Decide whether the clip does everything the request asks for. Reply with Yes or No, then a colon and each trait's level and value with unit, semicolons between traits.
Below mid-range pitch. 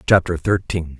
Yes: very low, 85 Hz